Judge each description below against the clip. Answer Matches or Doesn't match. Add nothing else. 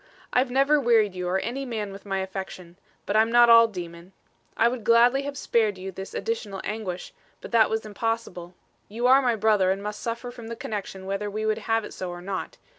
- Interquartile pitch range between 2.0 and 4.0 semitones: Matches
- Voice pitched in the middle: Doesn't match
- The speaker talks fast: Matches